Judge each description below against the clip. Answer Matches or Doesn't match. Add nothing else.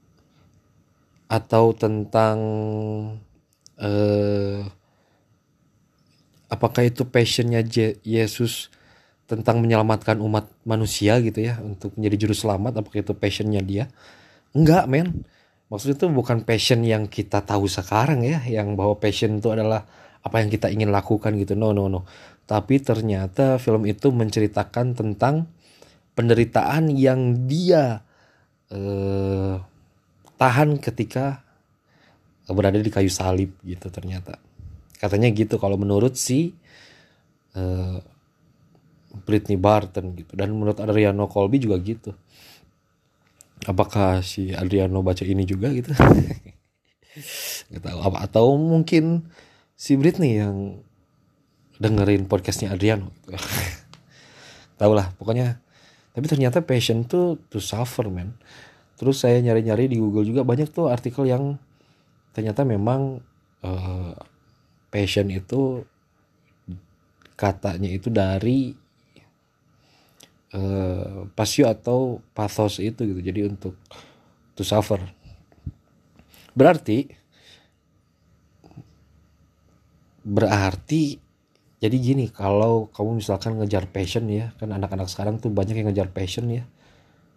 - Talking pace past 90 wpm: Matches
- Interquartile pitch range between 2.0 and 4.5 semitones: Matches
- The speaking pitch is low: Matches